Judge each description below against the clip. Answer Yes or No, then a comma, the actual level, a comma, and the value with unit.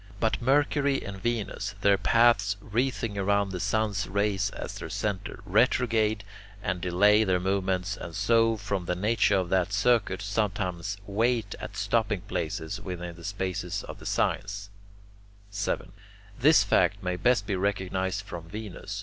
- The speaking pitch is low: Yes, low, 100 Hz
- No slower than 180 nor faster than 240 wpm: No, average, 150 wpm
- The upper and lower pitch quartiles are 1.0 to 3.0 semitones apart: Yes, narrow, 2.5 semitones